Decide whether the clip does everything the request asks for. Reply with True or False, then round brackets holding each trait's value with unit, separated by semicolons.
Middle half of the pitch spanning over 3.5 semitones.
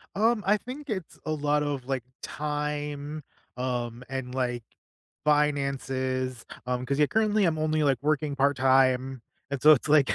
False (2.8 semitones)